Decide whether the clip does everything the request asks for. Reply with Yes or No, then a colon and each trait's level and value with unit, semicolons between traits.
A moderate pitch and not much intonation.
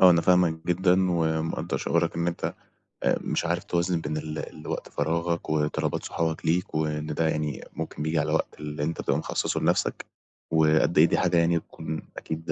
No: very low, 80 Hz; narrow, 1.7 semitones